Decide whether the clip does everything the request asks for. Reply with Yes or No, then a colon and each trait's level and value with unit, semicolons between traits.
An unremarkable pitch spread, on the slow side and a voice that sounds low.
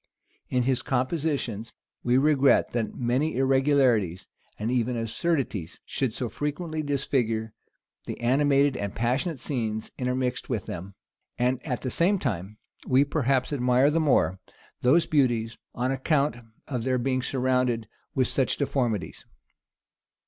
Yes: average, 3.1 semitones; slow, 130 wpm; low, 130 Hz